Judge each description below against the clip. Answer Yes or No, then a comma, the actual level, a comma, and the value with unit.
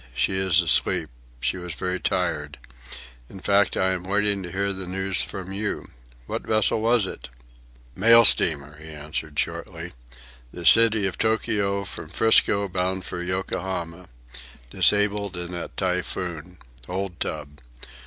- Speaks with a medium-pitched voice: No, very low, 95 Hz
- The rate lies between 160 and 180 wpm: No, average, 140 wpm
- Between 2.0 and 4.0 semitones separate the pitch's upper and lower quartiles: Yes, narrow, 2.4 semitones